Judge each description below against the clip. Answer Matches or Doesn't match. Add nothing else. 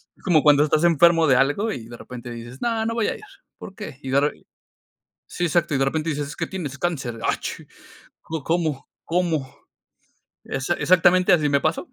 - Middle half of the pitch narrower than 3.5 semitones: Doesn't match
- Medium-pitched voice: Matches